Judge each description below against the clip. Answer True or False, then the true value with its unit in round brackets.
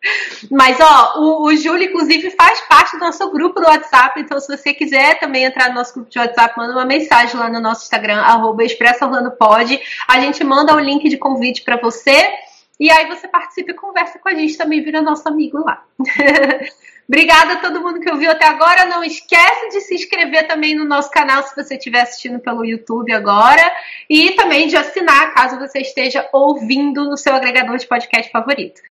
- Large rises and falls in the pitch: False (4.3 semitones)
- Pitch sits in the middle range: False (285 Hz)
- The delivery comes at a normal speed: False (195 wpm)